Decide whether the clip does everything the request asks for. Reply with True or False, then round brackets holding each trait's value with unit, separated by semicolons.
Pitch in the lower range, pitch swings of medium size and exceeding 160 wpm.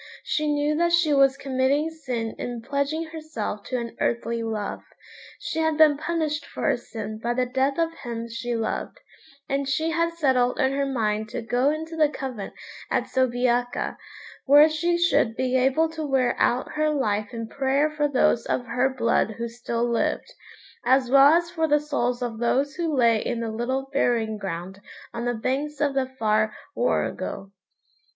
False (260 Hz; 4.3 semitones; 180 wpm)